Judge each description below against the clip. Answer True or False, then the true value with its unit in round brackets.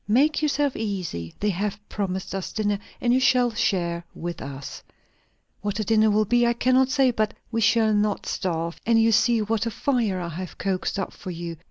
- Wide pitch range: False (4.2 semitones)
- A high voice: True (210 Hz)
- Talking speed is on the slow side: False (200 wpm)